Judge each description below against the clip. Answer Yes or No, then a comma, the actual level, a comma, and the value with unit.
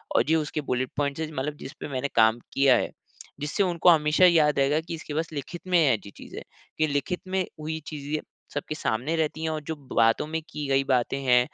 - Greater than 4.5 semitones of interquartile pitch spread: No, average, 2.7 semitones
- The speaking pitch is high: No, medium, 150 Hz